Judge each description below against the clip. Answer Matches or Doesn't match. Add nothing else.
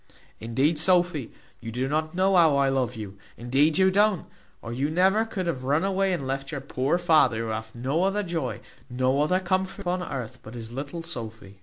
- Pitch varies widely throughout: Matches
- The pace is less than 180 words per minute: Doesn't match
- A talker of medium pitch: Matches